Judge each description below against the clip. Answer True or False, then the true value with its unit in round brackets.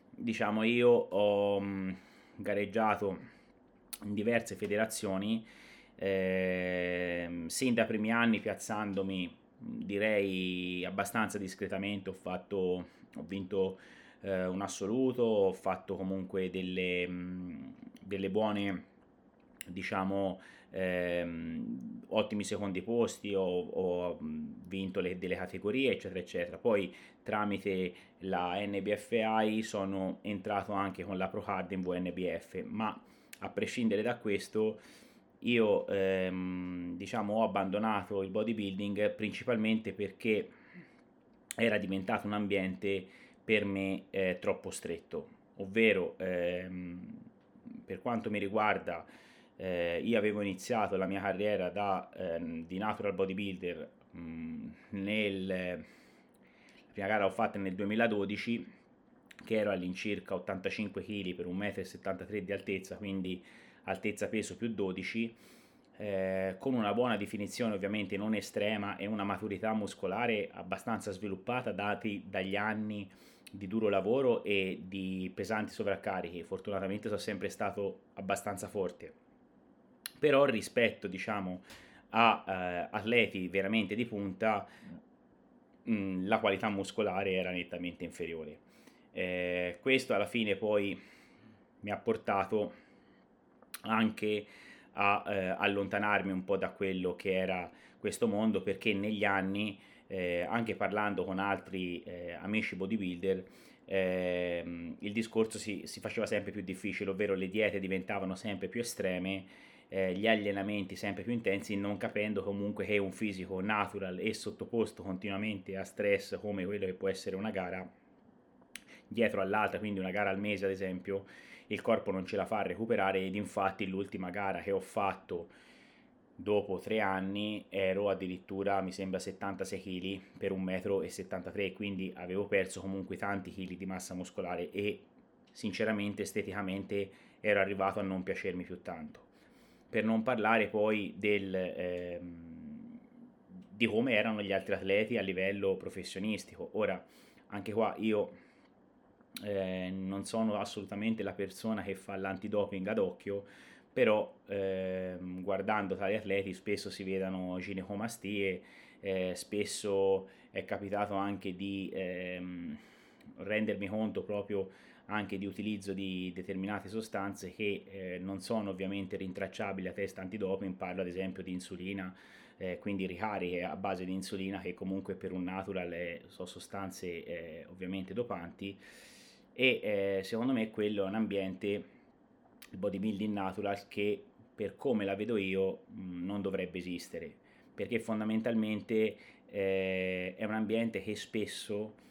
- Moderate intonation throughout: False (1.8 semitones)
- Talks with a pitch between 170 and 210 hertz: False (100 Hz)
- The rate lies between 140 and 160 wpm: False (125 wpm)